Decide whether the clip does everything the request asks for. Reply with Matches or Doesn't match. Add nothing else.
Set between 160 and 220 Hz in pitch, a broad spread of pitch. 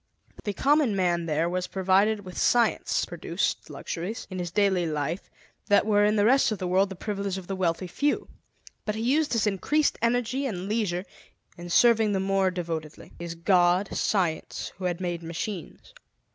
Doesn't match